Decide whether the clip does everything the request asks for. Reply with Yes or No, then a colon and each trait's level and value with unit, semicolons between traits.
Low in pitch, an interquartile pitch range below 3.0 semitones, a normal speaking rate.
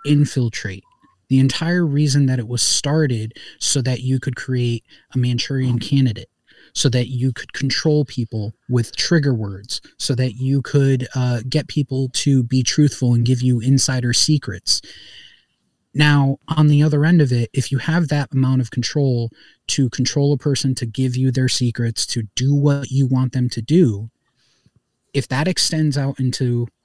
Yes: low, 130 Hz; narrow, 2.6 semitones; average, 170 wpm